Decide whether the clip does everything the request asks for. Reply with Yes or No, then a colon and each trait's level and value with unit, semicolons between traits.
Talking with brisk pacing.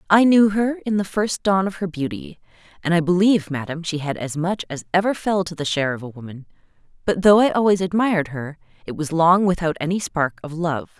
Yes: fast, 225 wpm